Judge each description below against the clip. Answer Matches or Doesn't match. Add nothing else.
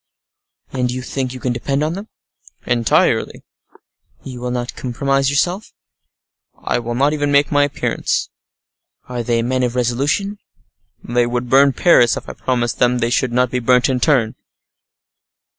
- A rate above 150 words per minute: Matches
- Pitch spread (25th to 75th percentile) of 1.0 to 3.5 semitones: Matches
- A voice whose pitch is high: Doesn't match